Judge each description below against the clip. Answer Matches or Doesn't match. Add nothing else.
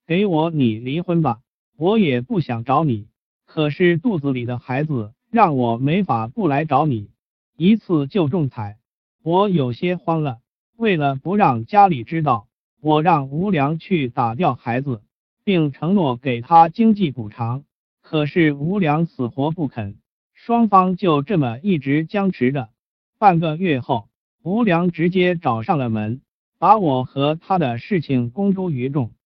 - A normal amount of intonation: Doesn't match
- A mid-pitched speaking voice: Matches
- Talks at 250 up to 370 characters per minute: Doesn't match